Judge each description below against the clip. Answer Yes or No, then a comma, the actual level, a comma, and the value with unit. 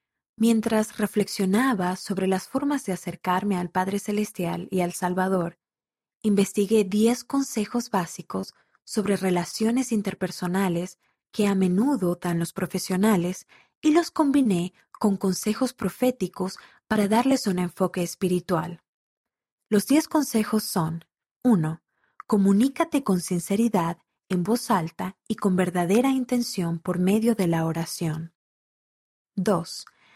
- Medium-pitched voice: No, high, 195 Hz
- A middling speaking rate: No, slow, 115 wpm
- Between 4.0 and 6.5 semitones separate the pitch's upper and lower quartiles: No, average, 3.6 semitones